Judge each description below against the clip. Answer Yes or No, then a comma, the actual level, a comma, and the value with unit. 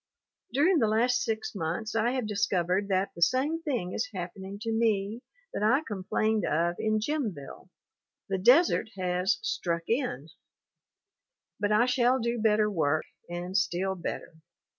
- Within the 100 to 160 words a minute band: Yes, average, 150 wpm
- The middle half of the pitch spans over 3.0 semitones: Yes, average, 4.5 semitones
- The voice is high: Yes, high, 210 Hz